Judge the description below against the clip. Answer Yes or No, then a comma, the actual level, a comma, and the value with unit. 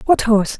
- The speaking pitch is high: Yes, high, 235 Hz